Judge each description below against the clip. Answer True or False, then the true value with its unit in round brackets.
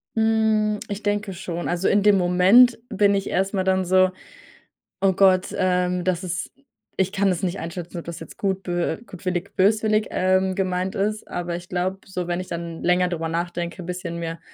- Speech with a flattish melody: True (2.1 semitones)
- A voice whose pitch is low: False (185 Hz)